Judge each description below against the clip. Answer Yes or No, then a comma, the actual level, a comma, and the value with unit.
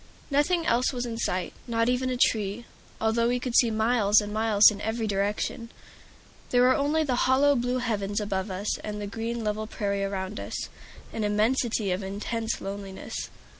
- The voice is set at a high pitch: Yes, high, 220 Hz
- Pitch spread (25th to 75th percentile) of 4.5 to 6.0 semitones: No, average, 3.2 semitones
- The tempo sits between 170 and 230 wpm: Yes, average, 175 wpm